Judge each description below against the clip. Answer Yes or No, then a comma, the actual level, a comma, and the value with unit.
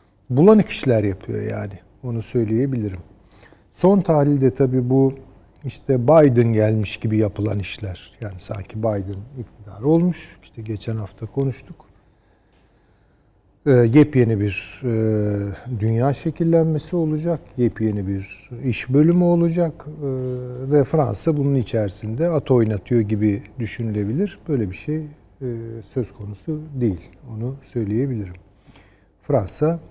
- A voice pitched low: Yes, low, 115 Hz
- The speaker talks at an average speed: Yes, average, 110 wpm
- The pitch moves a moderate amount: Yes, average, 5.0 semitones